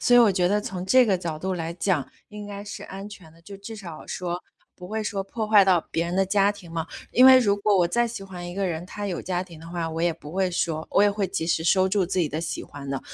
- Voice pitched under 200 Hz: Yes, medium, 185 Hz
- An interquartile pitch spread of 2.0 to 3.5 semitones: Yes, average, 3.1 semitones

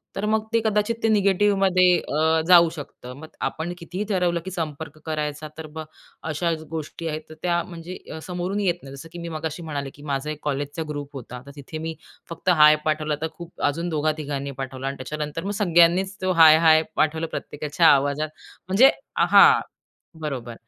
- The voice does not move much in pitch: No, average, 3.0 semitones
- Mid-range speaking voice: Yes, medium, 160 Hz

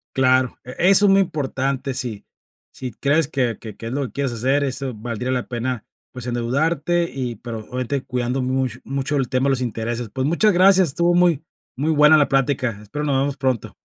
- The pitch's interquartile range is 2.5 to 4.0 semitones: Yes, average, 2.9 semitones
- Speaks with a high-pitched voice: No, low, 130 Hz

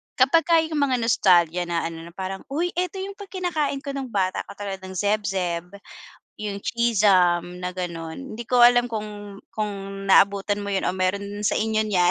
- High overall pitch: Yes, high, 205 Hz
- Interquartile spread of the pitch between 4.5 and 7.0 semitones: Yes, average, 4.8 semitones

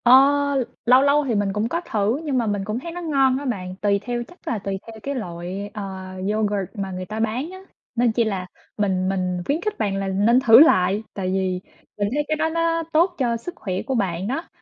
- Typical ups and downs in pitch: No, wide, 5.9 semitones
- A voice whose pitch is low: No, high, 220 Hz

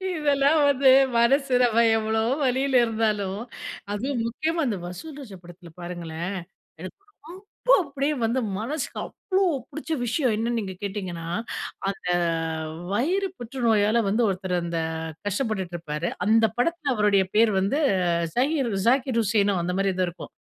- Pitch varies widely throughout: Yes, wide, 6.1 semitones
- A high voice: Yes, high, 225 Hz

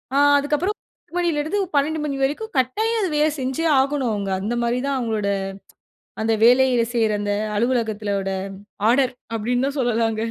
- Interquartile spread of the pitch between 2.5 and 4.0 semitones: No, average, 4.8 semitones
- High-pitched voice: Yes, very high, 255 Hz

